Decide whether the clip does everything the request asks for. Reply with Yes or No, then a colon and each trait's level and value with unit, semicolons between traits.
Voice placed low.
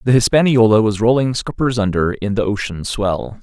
Yes: low, 110 Hz